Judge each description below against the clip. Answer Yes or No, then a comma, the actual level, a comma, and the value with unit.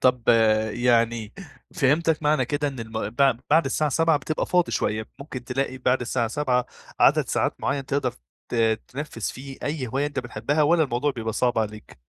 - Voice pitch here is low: Yes, low, 130 Hz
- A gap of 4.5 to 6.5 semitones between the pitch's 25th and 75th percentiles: No, average, 3.8 semitones